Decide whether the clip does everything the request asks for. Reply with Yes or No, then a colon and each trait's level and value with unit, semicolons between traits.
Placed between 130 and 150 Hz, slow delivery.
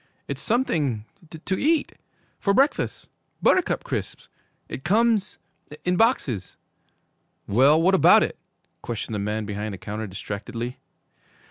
Yes: low, 135 Hz; slow, 120 wpm